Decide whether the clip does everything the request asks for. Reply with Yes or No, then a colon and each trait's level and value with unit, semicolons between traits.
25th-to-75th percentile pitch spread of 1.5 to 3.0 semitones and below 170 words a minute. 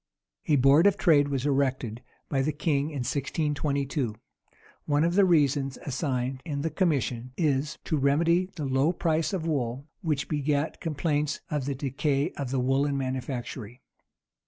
Yes: narrow, 2.6 semitones; average, 155 wpm